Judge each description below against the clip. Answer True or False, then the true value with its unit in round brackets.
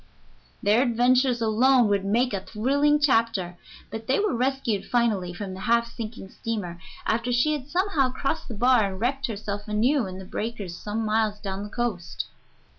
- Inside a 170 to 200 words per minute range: True (175 wpm)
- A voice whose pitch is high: True (230 Hz)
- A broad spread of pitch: False (3.8 semitones)